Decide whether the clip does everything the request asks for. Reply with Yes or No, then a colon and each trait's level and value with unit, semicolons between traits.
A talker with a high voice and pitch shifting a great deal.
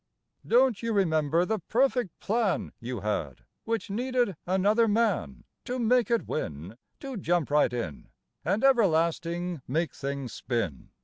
No: medium, 180 Hz; wide, 8.4 semitones